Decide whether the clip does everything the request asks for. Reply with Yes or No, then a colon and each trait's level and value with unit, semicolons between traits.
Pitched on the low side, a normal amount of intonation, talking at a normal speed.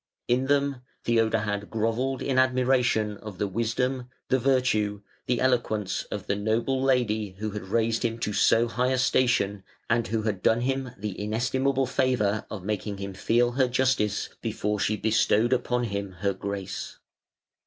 Yes: low, 115 Hz; average, 3.5 semitones; average, 160 wpm